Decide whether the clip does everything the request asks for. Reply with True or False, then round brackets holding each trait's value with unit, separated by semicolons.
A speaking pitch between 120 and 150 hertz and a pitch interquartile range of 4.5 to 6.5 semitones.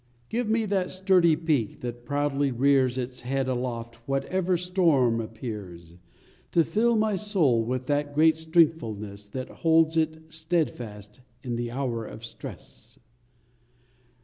True (140 Hz; 5.6 semitones)